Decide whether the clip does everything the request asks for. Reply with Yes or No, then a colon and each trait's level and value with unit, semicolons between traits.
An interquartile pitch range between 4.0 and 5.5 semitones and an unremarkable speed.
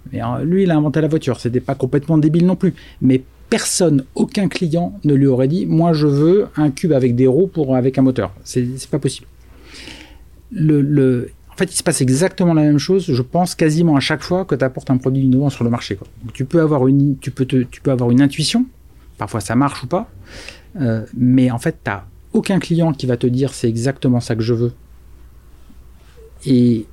No: average, 4.4 semitones; fast, 225 wpm